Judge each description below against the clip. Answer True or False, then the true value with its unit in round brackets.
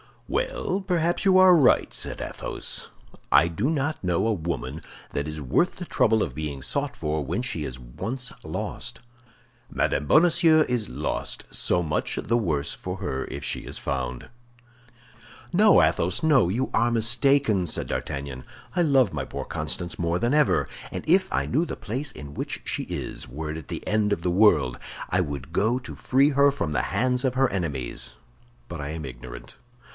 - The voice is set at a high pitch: False (105 Hz)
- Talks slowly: False (180 wpm)